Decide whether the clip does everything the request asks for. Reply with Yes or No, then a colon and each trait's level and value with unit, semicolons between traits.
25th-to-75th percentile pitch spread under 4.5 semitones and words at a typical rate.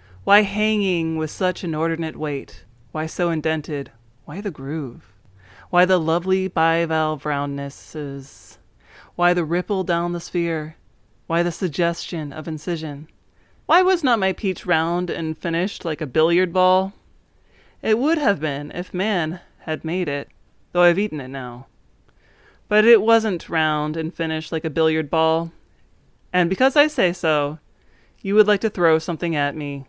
Yes: average, 3.7 semitones; average, 155 wpm